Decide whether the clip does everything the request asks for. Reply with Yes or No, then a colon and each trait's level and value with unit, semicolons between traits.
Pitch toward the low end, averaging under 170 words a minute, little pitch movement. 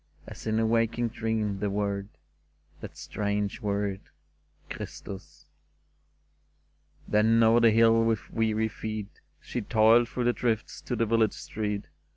Yes: low, 110 Hz; average, 150 wpm; narrow, 1.8 semitones